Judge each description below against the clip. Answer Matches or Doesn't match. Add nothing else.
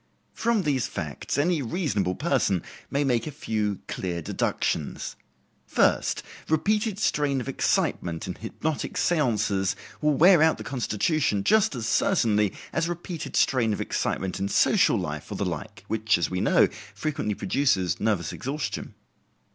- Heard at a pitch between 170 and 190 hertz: Doesn't match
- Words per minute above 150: Doesn't match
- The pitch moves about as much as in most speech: Doesn't match